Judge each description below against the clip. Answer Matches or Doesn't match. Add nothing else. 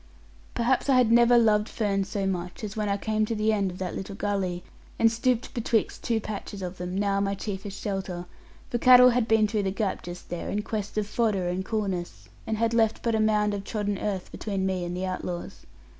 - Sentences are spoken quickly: Matches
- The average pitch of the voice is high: Matches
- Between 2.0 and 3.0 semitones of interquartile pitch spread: Matches